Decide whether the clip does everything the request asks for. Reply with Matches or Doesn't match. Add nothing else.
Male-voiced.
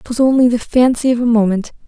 Doesn't match